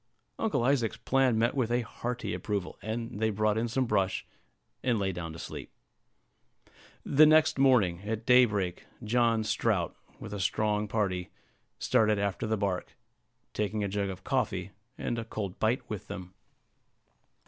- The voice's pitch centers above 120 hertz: No, low, 110 Hz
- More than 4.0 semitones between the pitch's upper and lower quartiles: No, average, 3.1 semitones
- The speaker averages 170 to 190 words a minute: No, average, 155 wpm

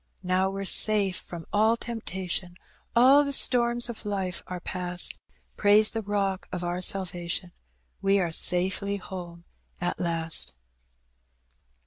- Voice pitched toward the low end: No, high, 190 Hz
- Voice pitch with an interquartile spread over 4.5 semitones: No, average, 2.9 semitones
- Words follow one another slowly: Yes, slow, 125 wpm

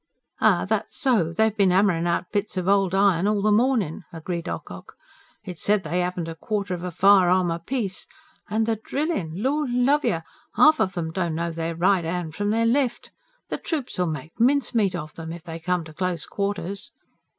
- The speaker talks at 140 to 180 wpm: No, average, 195 wpm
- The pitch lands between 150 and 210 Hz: Yes, high, 190 Hz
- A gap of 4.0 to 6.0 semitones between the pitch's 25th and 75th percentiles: Yes, average, 4.3 semitones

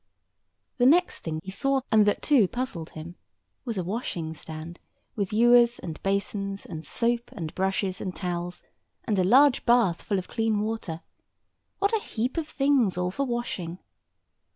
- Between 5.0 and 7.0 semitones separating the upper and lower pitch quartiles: Yes, wide, 5.4 semitones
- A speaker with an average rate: Yes, average, 160 wpm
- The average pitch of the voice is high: Yes, high, 205 Hz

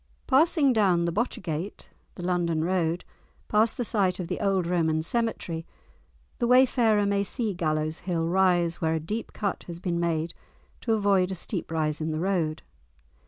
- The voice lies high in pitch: No, medium, 180 Hz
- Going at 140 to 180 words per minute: Yes, average, 165 wpm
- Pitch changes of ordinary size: Yes, average, 4.0 semitones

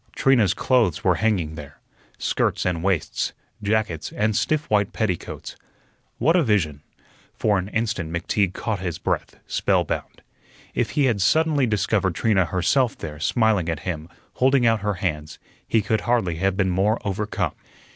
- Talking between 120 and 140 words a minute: No, average, 155 wpm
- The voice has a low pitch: Yes, low, 100 Hz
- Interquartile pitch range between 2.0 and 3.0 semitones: No, average, 4.3 semitones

